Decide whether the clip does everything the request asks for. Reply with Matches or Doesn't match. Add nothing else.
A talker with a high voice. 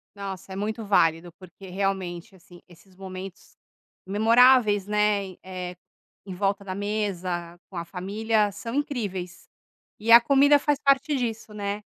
Matches